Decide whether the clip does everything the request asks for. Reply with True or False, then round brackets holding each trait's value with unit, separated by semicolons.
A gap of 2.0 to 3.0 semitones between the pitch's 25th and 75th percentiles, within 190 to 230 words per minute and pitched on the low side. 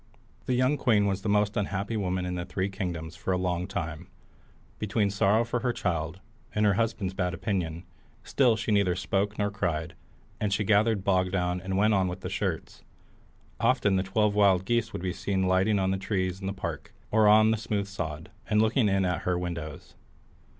True (2.7 semitones; 200 wpm; 95 Hz)